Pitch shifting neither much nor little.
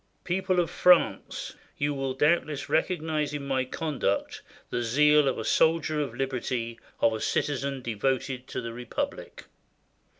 Yes: average, 3.4 semitones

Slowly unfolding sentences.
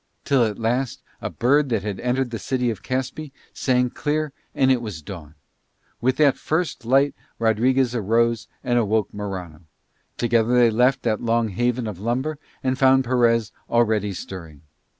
No: average, 160 wpm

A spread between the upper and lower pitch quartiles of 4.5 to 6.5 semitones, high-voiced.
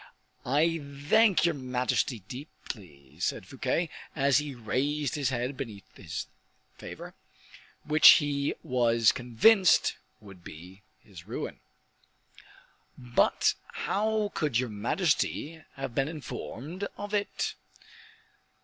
No: average, 5.1 semitones; low, 135 Hz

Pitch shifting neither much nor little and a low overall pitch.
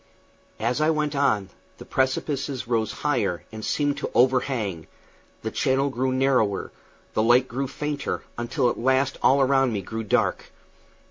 Yes: average, 3.5 semitones; low, 130 Hz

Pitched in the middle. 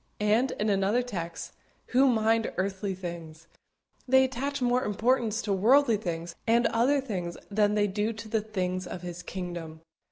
No: high, 210 Hz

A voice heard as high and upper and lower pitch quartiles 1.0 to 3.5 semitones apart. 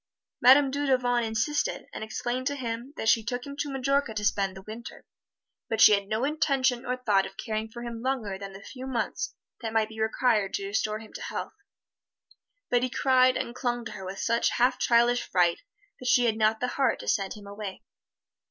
Yes: high, 235 Hz; average, 2.9 semitones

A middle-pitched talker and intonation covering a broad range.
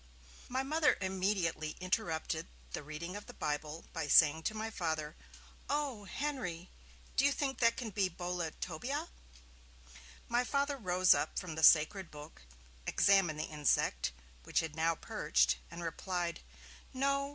Yes: medium, 180 Hz; wide, 7.0 semitones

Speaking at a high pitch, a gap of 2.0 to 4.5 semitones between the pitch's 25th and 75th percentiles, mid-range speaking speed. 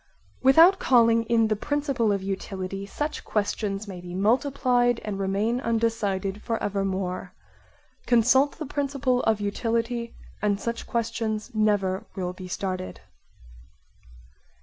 No: high, 220 Hz; average, 3.7 semitones; slow, 120 wpm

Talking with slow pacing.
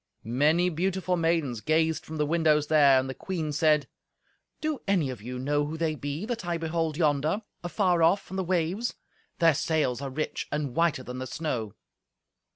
No: average, 180 wpm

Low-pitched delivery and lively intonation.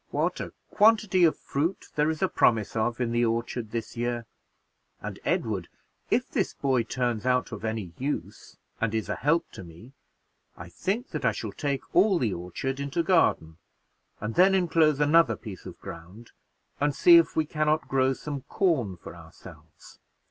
Yes: low, 130 Hz; wide, 6.1 semitones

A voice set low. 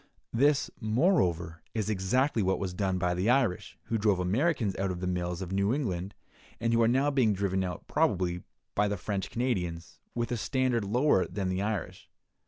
Yes: low, 100 Hz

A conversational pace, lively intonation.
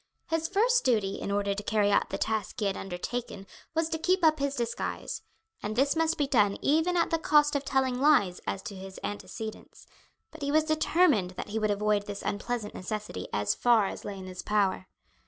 No: fast, 210 wpm; wide, 7.0 semitones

